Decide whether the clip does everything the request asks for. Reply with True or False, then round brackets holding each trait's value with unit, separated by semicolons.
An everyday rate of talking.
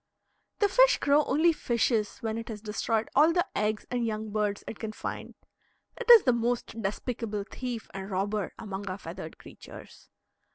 True (170 wpm)